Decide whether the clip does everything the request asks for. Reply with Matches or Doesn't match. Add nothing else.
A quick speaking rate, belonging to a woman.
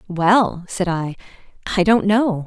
Doesn't match